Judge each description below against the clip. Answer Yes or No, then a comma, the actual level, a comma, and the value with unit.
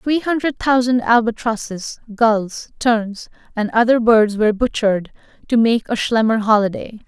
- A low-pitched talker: No, high, 225 Hz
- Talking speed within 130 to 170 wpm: Yes, slow, 135 wpm